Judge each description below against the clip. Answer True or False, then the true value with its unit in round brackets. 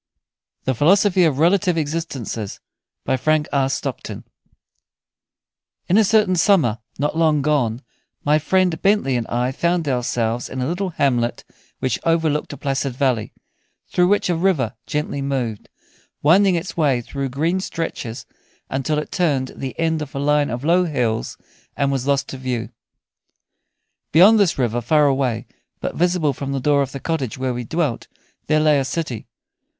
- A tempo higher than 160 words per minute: False (155 wpm)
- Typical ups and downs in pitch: True (4.3 semitones)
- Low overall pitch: False (145 Hz)